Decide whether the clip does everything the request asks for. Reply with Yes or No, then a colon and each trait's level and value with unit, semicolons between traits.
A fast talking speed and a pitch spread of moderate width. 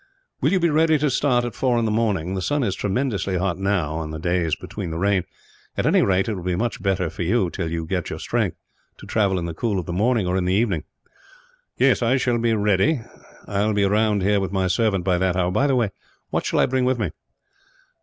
Yes: fast, 245 wpm; average, 4.6 semitones